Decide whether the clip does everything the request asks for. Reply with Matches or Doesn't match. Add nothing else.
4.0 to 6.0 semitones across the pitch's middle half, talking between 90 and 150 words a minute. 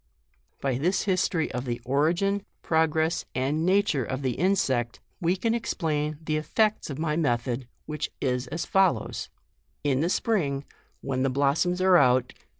Doesn't match